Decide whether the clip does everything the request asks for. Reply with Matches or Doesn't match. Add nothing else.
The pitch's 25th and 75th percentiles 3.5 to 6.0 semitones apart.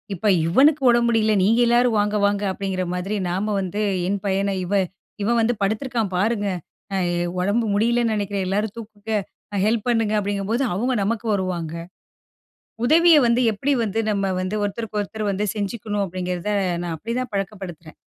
Doesn't match